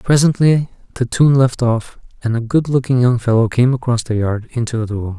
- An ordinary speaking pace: No, fast, 210 wpm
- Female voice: No, male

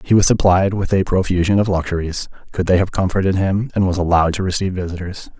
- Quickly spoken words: Yes, fast, 210 wpm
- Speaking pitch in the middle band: No, very low, 95 Hz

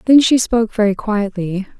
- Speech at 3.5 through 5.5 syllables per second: Yes, 5.2 syllables/s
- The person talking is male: No, female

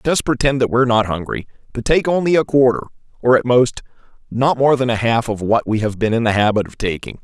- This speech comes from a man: Yes, male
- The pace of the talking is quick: Yes, fast, 240 wpm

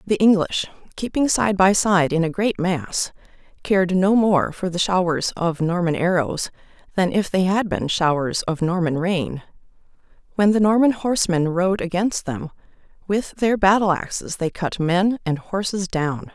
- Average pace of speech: Yes, average, 165 wpm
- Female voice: Yes, female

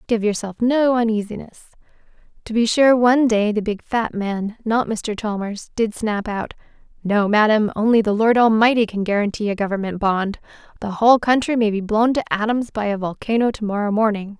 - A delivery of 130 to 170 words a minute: No, average, 180 wpm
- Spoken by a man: No, female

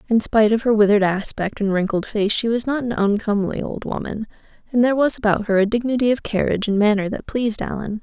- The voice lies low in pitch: No, high, 215 Hz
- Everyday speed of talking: No, fast, 225 wpm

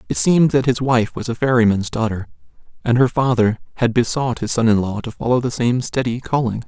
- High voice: No, low, 120 Hz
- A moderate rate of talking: No, fast, 215 wpm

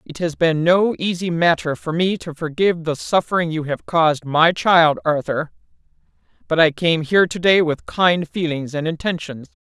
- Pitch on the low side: No, medium, 165 Hz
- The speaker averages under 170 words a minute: No, average, 180 wpm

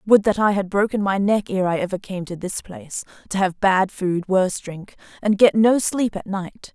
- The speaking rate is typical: No, fast, 230 wpm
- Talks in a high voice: Yes, high, 195 Hz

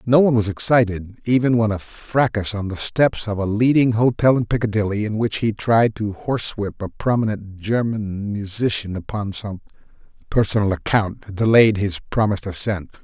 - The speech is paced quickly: No, average, 165 wpm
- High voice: No, low, 105 Hz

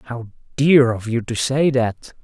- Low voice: Yes, low, 125 Hz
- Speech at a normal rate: Yes, average, 190 wpm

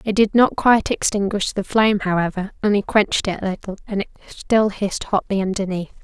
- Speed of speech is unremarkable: Yes, average, 170 wpm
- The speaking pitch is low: No, high, 200 Hz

